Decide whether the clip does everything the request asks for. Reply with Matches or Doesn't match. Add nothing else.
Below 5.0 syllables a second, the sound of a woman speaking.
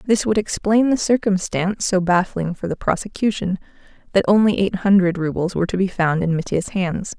Doesn't match